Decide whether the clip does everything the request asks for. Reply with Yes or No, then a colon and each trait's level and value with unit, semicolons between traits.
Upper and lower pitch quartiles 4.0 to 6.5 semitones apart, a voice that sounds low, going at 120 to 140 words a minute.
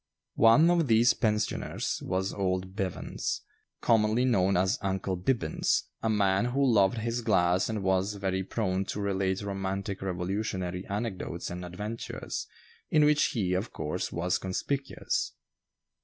No: average, 3.3 semitones; low, 100 Hz; slow, 135 wpm